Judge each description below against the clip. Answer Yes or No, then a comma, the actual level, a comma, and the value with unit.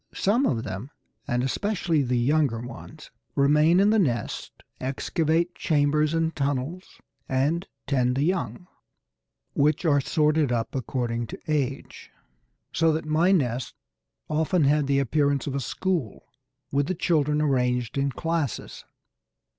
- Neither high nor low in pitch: Yes, medium, 145 Hz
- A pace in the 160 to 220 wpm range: No, slow, 135 wpm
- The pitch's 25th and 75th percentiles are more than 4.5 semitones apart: No, average, 3.8 semitones